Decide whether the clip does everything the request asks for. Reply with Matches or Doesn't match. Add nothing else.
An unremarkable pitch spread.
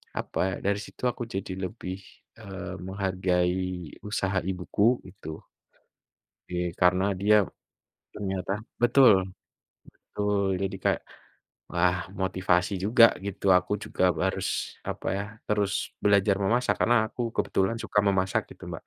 Doesn't match